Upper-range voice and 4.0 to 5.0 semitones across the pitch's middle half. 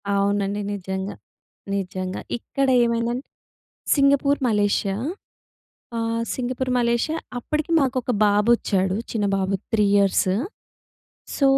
Yes: high, 215 Hz; average, 4.4 semitones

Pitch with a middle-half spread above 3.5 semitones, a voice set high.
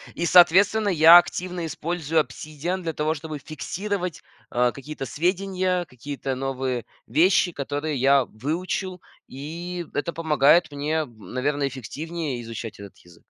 No: average, 4.3 semitones; medium, 155 Hz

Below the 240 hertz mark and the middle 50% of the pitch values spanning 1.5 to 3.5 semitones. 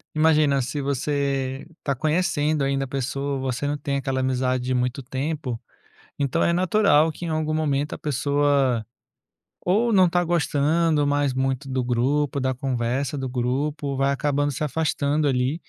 Yes: medium, 140 Hz; narrow, 2.5 semitones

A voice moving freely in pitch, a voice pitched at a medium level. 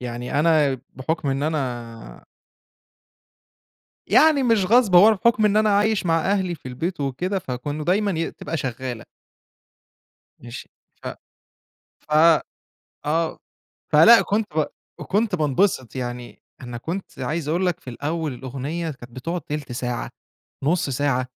Yes: wide, 6.2 semitones; medium, 155 Hz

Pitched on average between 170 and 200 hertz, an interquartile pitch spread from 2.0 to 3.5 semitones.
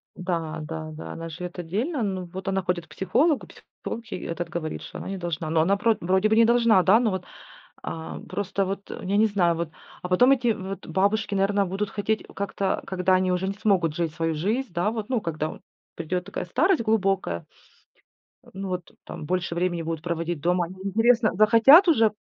No: high, 190 Hz; average, 3.9 semitones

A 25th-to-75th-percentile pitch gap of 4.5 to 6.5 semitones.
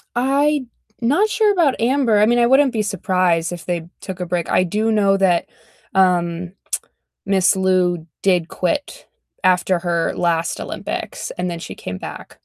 Yes: wide, 5.6 semitones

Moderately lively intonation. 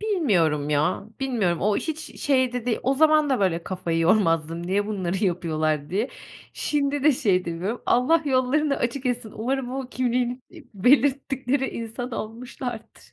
No: wide, 6.6 semitones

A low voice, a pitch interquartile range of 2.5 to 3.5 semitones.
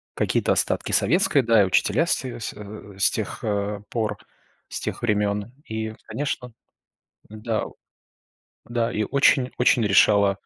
Yes: low, 110 Hz; average, 2.9 semitones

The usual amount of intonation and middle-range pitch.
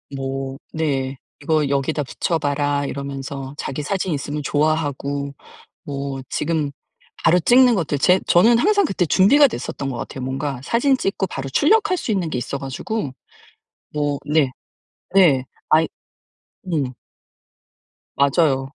Yes: average, 4.7 semitones; medium, 145 Hz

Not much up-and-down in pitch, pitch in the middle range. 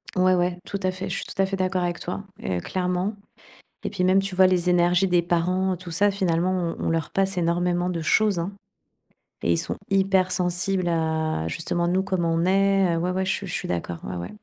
Yes: narrow, 1.9 semitones; medium, 180 Hz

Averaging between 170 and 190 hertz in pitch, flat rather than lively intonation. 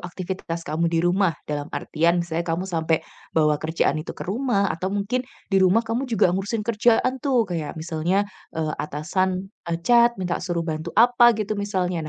No: medium, 185 Hz; average, 4.2 semitones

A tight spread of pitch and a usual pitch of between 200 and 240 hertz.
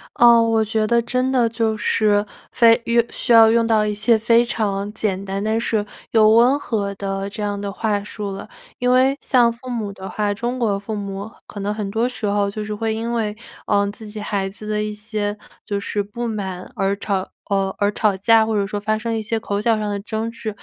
Yes: narrow, 2.1 semitones; high, 215 Hz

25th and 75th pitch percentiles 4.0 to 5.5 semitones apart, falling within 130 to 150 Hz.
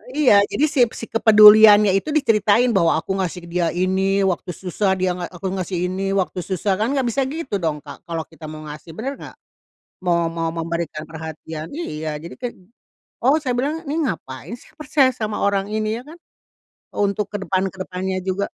No: average, 4.8 semitones; high, 190 Hz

